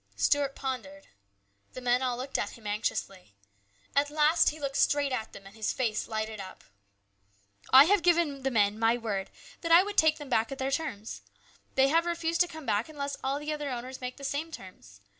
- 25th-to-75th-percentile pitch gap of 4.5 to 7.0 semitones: Yes, average, 5.3 semitones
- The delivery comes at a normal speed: No, fast, 210 wpm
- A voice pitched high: Yes, very high, 265 Hz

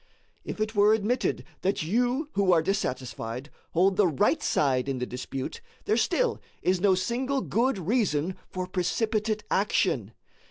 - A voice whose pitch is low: No, high, 190 Hz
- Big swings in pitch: Yes, wide, 5.9 semitones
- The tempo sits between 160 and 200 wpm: No, average, 150 wpm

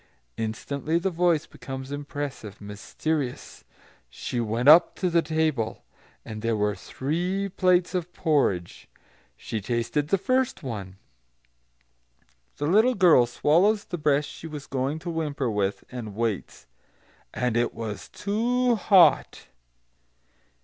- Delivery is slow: Yes, slow, 125 wpm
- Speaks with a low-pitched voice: No, medium, 145 Hz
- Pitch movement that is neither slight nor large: No, wide, 7.1 semitones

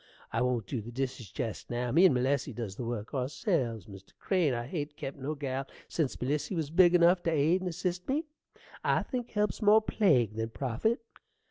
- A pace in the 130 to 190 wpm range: No, average, 200 wpm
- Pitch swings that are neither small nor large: No, wide, 6.8 semitones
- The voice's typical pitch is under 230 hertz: Yes, medium, 140 Hz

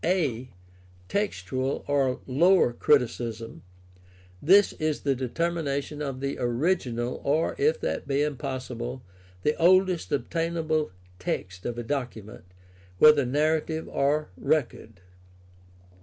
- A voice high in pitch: No, medium, 140 Hz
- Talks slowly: Yes, slow, 110 wpm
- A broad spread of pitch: No, average, 4.6 semitones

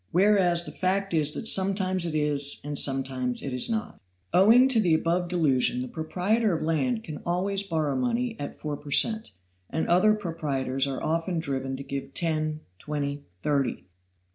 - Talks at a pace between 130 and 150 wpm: No, average, 170 wpm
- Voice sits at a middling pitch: Yes, medium, 165 Hz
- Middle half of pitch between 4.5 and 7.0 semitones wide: Yes, average, 5.2 semitones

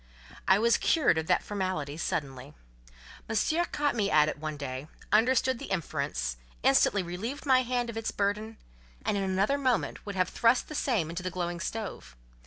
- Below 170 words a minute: No, average, 180 wpm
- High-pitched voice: Yes, high, 195 Hz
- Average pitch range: No, wide, 6.8 semitones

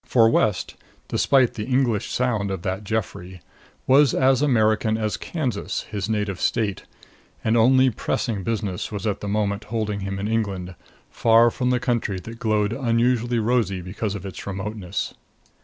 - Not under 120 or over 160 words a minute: Yes, average, 155 wpm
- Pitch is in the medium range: No, low, 110 Hz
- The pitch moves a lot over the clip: No, average, 2.9 semitones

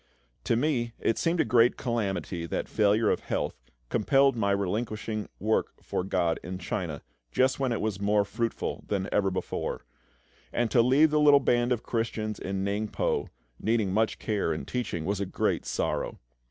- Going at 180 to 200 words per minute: No, average, 170 wpm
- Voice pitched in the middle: No, low, 110 Hz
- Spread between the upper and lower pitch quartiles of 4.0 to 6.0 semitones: No, average, 3.4 semitones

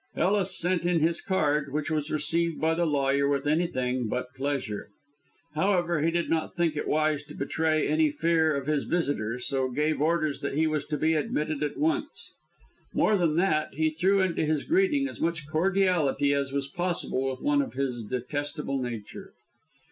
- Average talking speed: Yes, average, 180 wpm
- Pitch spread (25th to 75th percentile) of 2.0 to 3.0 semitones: No, average, 3.5 semitones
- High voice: No, medium, 155 Hz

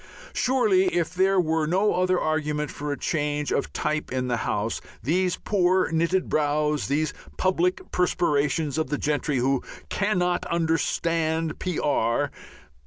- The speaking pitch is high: No, medium, 160 Hz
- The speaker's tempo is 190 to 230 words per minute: No, slow, 135 wpm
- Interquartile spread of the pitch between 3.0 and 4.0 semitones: Yes, average, 3.6 semitones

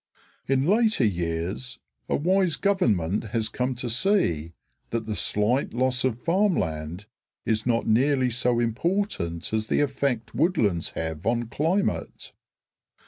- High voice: No, low, 120 Hz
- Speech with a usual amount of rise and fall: No, wide, 5.9 semitones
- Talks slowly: Yes, slow, 130 wpm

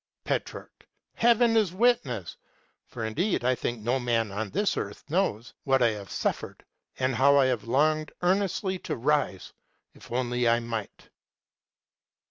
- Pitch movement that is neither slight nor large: No, wide, 7.4 semitones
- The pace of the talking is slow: No, average, 145 wpm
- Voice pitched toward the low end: Yes, low, 130 Hz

